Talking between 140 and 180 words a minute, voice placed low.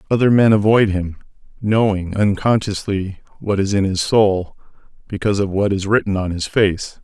Yes: average, 160 wpm; low, 100 Hz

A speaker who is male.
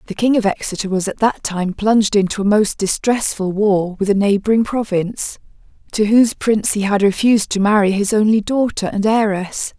No: female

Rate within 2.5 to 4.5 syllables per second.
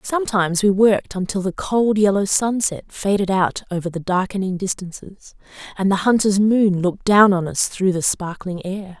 No: 5.0 syllables/s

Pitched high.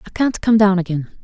Yes: high, 195 Hz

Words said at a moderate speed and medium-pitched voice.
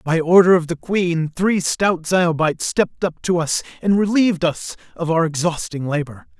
Yes: average, 180 wpm; medium, 170 Hz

